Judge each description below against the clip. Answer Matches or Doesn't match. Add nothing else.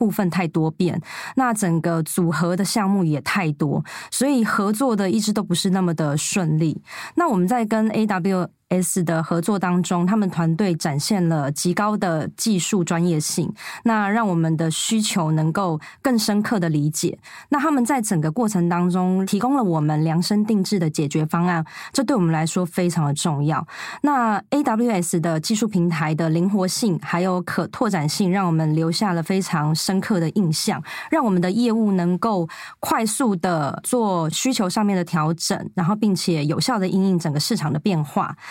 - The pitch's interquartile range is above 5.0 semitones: Doesn't match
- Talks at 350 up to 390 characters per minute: Doesn't match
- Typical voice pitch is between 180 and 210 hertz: Matches